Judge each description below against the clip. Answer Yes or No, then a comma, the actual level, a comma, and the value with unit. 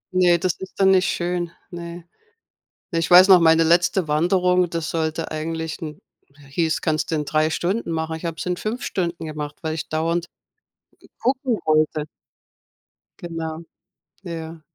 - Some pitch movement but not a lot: No, narrow, 2.0 semitones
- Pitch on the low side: No, medium, 165 Hz